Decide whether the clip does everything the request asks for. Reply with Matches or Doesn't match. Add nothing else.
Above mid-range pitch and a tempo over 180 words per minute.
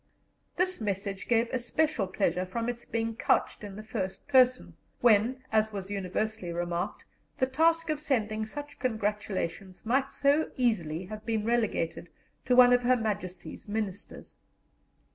Doesn't match